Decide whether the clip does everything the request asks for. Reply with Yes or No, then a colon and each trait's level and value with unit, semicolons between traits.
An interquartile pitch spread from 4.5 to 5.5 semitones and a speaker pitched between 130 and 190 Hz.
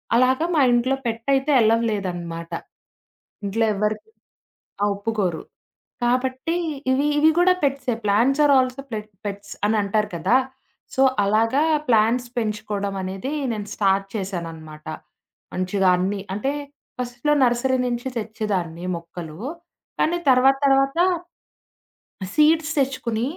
No: average, 4.9 semitones; high, 225 Hz